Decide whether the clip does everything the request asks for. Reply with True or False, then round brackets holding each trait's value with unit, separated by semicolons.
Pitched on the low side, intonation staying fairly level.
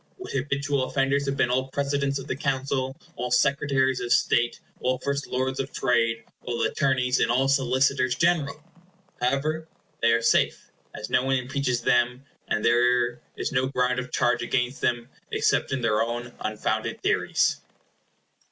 True (130 Hz; 2.1 semitones)